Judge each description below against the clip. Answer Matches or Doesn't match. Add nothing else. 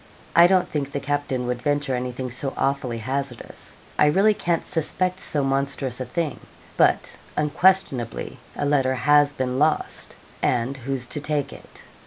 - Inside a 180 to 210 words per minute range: Doesn't match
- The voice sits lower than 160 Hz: Matches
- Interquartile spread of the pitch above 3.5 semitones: Doesn't match